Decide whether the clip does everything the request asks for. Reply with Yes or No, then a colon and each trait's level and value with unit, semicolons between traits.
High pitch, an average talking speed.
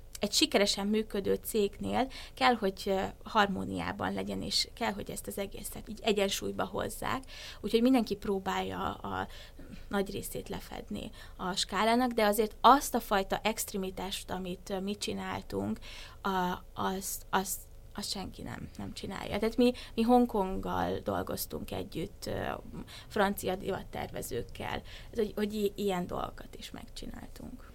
Yes: high, 195 Hz; average, 120 wpm